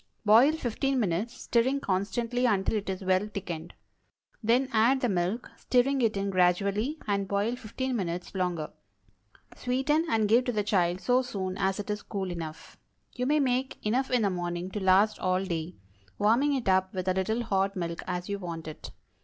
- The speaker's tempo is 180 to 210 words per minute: Yes, average, 185 wpm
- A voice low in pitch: No, high, 205 Hz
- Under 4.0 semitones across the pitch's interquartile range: No, average, 4.9 semitones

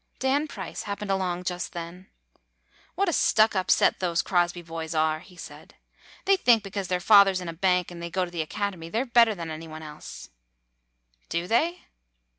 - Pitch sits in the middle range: Yes, medium, 180 Hz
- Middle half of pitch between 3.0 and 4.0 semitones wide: Yes, average, 3.7 semitones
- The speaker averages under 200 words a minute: No, fast, 205 wpm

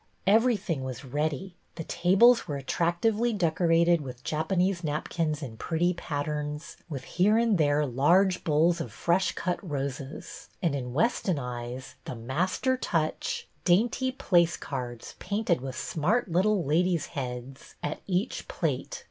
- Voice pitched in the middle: Yes, medium, 165 Hz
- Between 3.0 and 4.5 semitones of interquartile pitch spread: No, average, 5.0 semitones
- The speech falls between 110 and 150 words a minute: Yes, average, 145 wpm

